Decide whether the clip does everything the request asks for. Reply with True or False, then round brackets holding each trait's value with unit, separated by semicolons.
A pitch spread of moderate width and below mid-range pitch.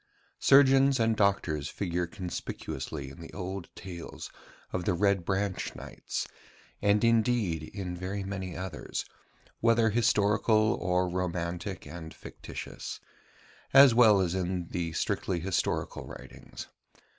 True (3.6 semitones; 95 Hz)